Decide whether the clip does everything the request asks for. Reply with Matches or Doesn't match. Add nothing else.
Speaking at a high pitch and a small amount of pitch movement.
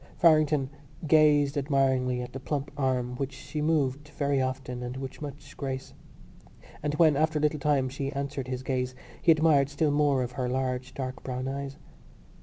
Doesn't match